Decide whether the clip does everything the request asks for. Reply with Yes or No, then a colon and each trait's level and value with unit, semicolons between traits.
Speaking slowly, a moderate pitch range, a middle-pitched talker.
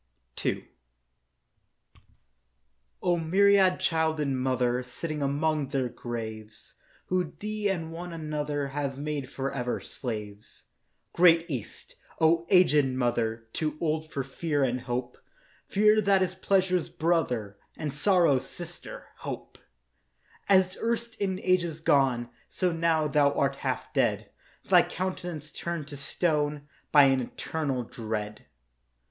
Yes: slow, 120 wpm; average, 4.9 semitones; medium, 150 Hz